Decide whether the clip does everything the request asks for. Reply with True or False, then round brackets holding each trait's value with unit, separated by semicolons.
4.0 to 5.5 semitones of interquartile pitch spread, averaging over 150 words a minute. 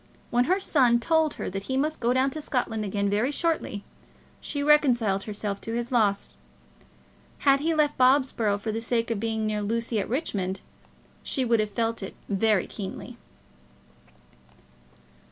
True (4.5 semitones; 160 wpm)